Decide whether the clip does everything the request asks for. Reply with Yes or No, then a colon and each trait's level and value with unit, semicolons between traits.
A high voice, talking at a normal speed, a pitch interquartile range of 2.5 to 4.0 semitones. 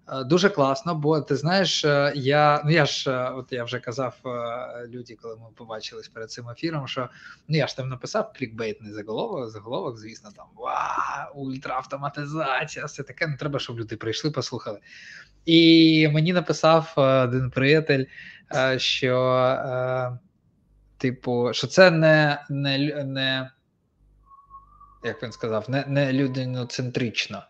No: low, 135 Hz; average, 130 wpm; average, 3.6 semitones